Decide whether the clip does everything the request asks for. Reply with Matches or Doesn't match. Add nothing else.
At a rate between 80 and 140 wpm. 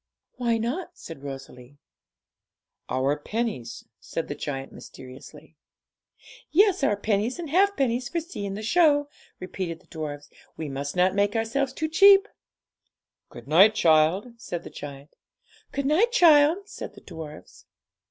Matches